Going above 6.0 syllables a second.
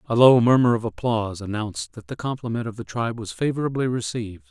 Yes: 6.5 syllables/s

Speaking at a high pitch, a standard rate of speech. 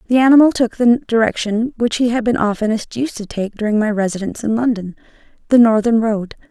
Yes: high, 225 Hz; average, 185 wpm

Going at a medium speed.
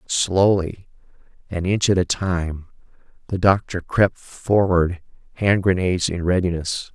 No: slow, 120 wpm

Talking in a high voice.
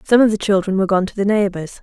Yes: high, 200 Hz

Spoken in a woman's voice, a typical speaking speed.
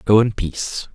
No: male; average, 190 wpm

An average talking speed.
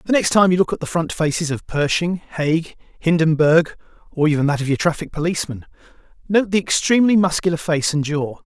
Yes: average, 190 wpm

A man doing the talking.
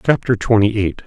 Yes: male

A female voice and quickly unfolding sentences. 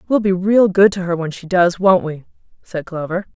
Yes: female; fast, 235 wpm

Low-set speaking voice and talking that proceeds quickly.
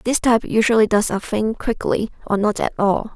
No: high, 215 Hz; fast, 210 wpm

